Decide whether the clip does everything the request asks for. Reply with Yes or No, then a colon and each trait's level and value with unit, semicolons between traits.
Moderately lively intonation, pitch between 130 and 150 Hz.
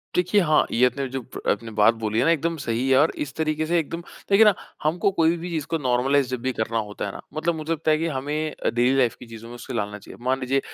Yes: average, 4.9 semitones; low, 135 Hz